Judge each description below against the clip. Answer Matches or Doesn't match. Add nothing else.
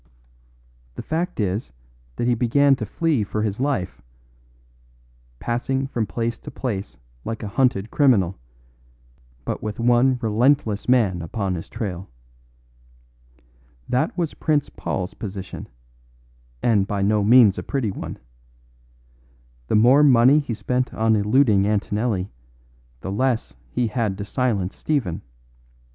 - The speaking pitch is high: Doesn't match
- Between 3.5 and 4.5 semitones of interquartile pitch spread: Matches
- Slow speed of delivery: Matches